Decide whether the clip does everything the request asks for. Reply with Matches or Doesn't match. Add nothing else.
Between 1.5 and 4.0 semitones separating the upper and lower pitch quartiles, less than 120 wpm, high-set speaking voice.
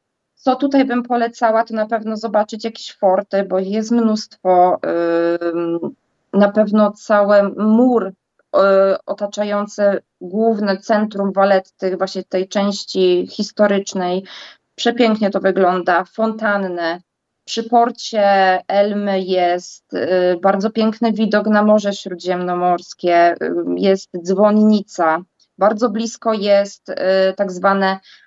Matches